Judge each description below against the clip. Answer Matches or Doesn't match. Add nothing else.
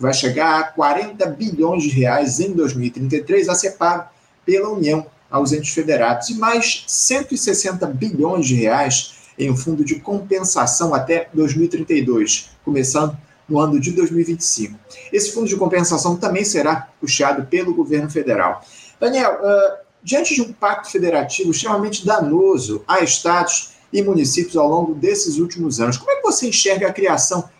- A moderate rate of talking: Matches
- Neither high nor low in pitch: Matches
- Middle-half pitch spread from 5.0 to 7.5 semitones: Matches